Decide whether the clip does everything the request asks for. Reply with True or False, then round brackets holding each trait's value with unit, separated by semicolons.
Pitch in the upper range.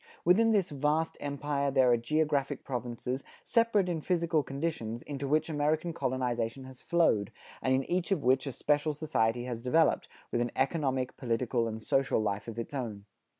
False (135 Hz)